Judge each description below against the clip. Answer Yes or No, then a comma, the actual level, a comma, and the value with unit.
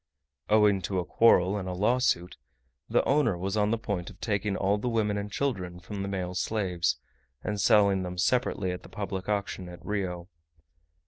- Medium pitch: No, low, 100 Hz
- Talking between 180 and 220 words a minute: Yes, average, 185 wpm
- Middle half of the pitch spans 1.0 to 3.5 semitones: Yes, narrow, 2.6 semitones